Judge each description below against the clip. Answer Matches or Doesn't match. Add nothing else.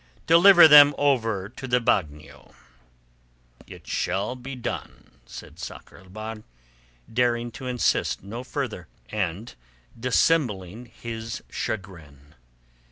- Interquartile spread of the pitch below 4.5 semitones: Doesn't match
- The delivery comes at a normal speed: Doesn't match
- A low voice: Matches